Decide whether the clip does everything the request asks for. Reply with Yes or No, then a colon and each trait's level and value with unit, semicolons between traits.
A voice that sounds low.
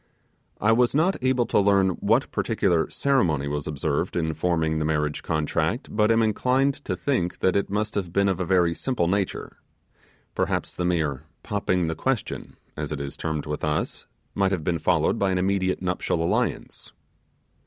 Yes: very low, 90 Hz